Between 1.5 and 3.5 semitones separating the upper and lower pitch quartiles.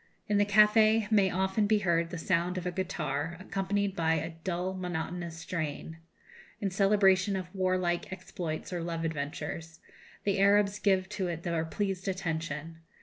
Yes: average, 3.0 semitones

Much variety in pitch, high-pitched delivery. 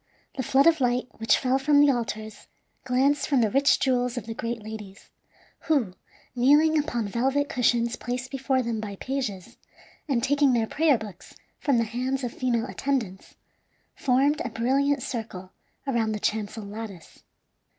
No: average, 3.6 semitones; high, 245 Hz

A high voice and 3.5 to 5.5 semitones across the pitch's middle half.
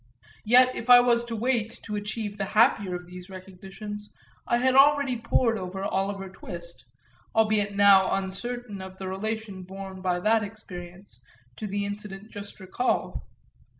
No: high, 205 Hz; average, 2.9 semitones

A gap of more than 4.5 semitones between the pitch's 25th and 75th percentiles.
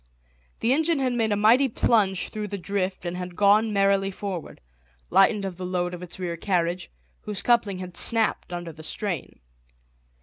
No: average, 3.1 semitones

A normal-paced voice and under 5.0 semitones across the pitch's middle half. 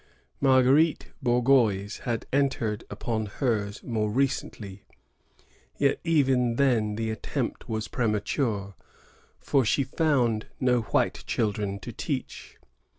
No: slow, 105 wpm; average, 3.9 semitones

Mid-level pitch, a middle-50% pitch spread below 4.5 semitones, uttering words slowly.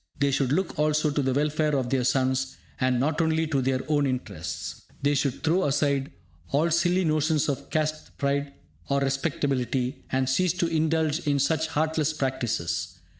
No: medium, 145 Hz; average, 2.8 semitones; average, 170 wpm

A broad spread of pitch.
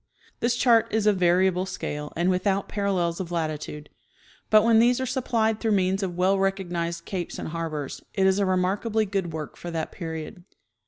No: average, 3.6 semitones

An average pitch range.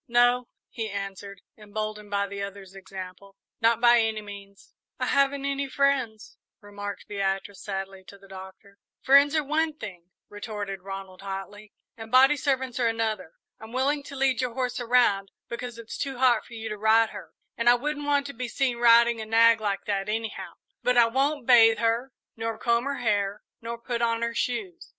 Yes: average, 3.8 semitones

